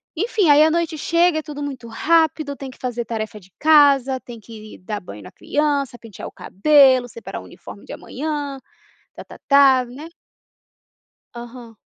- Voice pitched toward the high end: Yes, very high, 275 Hz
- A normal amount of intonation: Yes, average, 4.4 semitones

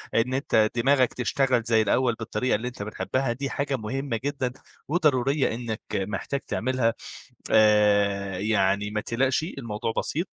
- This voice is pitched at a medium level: No, low, 120 Hz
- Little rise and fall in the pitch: No, average, 3.8 semitones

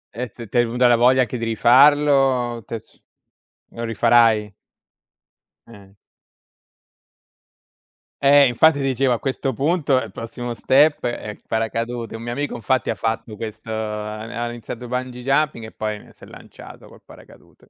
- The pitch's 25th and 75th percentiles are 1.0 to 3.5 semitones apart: Yes, average, 2.7 semitones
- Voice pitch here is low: Yes, low, 120 Hz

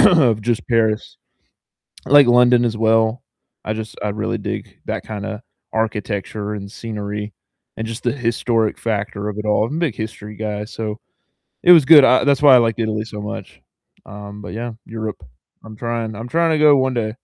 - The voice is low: Yes, low, 110 Hz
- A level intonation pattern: Yes, narrow, 2.3 semitones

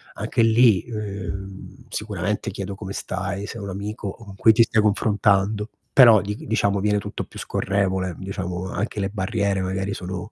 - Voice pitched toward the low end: Yes, low, 100 Hz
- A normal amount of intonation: No, narrow, 1.9 semitones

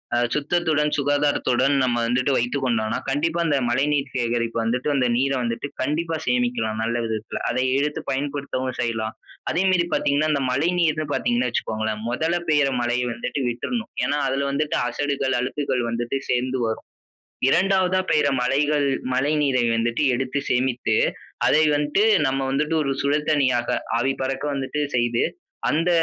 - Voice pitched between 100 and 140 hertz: Yes, low, 135 Hz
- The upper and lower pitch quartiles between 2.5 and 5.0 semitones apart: Yes, average, 3.4 semitones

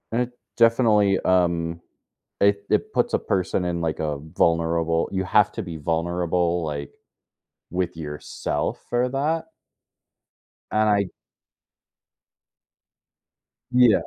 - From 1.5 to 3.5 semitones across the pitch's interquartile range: No, average, 4.2 semitones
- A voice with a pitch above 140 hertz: No, very low, 90 Hz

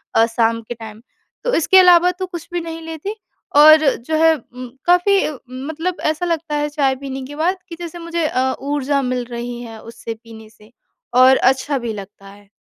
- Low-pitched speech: No, very high, 285 Hz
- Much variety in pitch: Yes, wide, 5.9 semitones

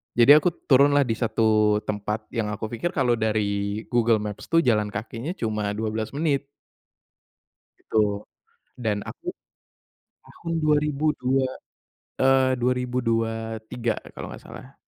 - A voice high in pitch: No, low, 115 Hz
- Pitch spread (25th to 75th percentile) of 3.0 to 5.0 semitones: Yes, average, 3.7 semitones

